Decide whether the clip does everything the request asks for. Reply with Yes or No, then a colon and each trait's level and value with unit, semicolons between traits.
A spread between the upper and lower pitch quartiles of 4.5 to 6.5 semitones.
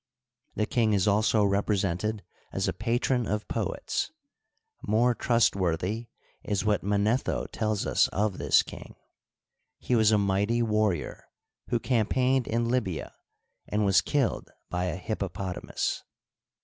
No: average, 2.9 semitones